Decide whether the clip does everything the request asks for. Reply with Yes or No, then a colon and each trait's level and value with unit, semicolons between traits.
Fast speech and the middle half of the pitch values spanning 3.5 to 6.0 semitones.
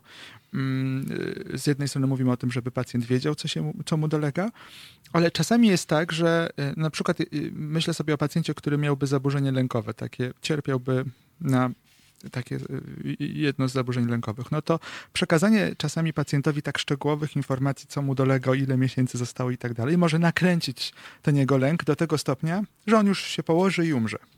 Yes: fast, 170 wpm; average, 3.9 semitones